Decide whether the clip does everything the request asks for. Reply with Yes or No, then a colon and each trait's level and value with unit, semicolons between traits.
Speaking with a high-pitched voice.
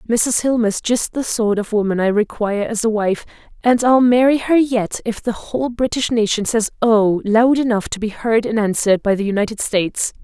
Yes: high, 225 Hz